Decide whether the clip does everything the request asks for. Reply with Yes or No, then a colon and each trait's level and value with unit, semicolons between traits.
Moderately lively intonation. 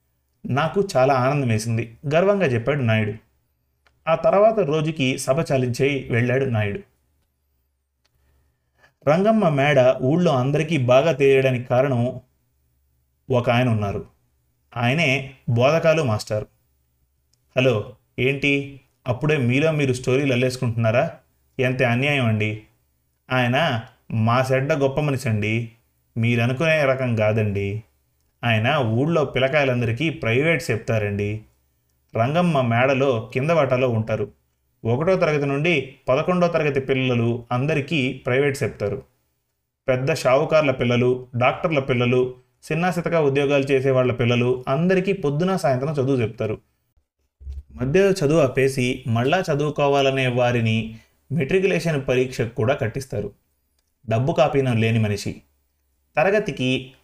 Yes: average, 4.3 semitones